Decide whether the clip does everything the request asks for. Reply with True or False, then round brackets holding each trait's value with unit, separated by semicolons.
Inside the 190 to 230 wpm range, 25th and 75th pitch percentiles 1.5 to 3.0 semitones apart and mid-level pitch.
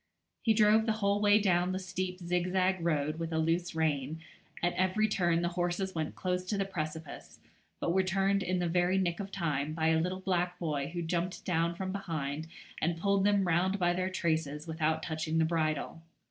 True (200 wpm; 2.7 semitones; 175 Hz)